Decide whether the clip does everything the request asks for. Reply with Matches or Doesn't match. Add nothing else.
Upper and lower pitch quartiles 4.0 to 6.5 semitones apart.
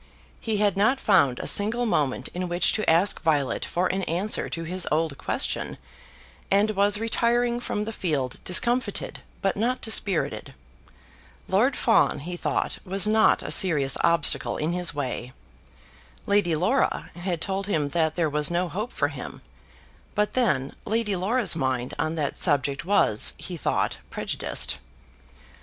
Matches